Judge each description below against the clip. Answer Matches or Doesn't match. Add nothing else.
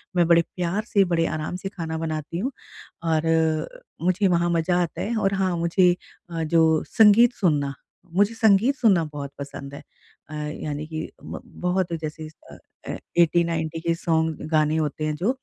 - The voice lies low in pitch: Doesn't match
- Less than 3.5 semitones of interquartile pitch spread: Matches